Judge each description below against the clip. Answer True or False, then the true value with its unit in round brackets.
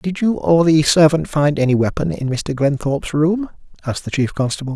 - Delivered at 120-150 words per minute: False (200 wpm)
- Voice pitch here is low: False (150 Hz)